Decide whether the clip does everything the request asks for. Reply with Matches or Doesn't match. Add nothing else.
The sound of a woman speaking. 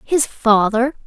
Matches